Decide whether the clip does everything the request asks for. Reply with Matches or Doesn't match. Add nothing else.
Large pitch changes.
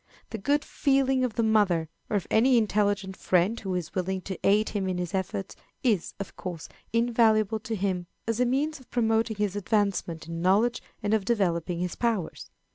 Doesn't match